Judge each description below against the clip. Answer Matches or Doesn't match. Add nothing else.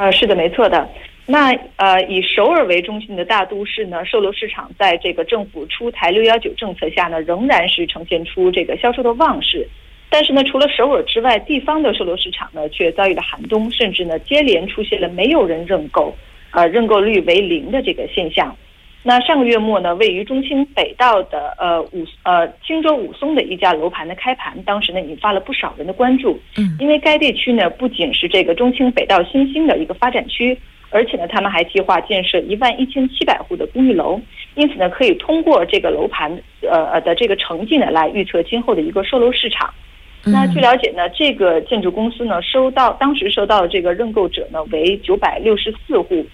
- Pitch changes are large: Matches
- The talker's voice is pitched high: Matches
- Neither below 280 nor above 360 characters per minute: Matches